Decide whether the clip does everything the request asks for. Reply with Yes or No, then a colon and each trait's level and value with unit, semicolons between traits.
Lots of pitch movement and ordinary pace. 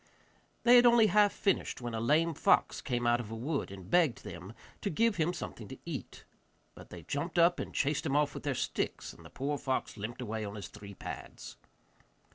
No: wide, 7.1 semitones; fast, 215 wpm